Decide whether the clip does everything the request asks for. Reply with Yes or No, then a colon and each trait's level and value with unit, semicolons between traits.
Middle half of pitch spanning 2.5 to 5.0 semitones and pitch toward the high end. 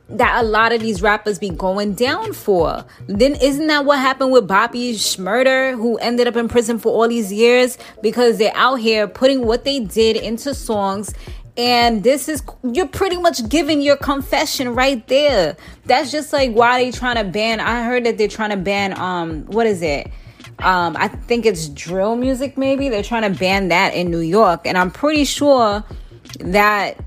Yes: average, 4.0 semitones; high, 235 Hz